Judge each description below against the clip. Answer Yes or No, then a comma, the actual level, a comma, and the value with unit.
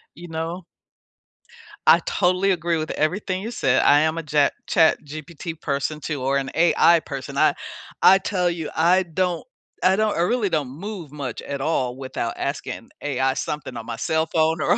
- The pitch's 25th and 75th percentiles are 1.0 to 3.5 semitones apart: No, average, 3.9 semitones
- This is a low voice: No, medium, 160 Hz